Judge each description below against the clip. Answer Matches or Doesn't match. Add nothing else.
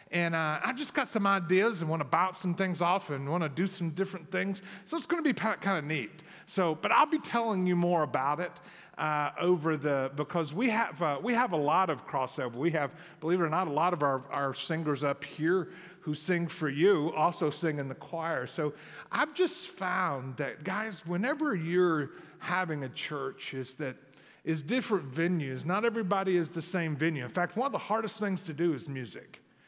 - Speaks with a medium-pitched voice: Matches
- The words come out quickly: Matches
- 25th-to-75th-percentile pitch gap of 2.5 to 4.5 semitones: Matches